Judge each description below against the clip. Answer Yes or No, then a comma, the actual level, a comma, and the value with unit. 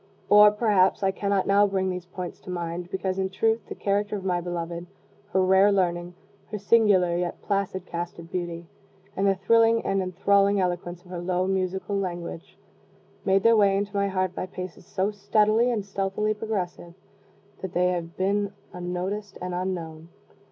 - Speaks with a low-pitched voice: No, high, 190 Hz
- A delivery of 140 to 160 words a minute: No, average, 175 wpm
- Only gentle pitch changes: Yes, narrow, 2.2 semitones